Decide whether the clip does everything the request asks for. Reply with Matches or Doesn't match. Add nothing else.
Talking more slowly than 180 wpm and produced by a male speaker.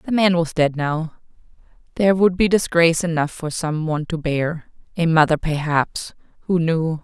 Doesn't match